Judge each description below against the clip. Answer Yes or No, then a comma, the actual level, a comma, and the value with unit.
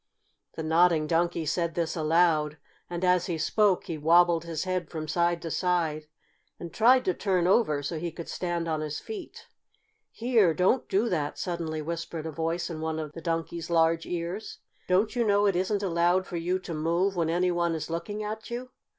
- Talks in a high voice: No, medium, 170 Hz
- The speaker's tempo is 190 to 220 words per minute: Yes, average, 195 wpm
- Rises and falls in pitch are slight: Yes, narrow, 2.2 semitones